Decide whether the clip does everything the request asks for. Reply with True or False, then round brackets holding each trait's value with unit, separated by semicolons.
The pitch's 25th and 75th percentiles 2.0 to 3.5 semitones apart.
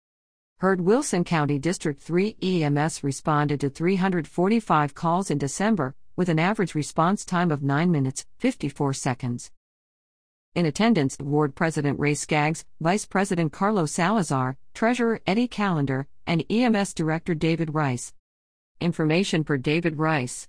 False (4.4 semitones)